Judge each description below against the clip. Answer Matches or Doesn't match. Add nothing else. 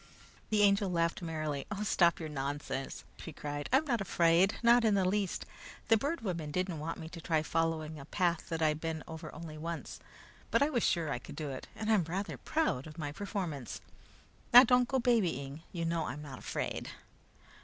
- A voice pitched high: Doesn't match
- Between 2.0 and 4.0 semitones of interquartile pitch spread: Doesn't match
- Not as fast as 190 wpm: Doesn't match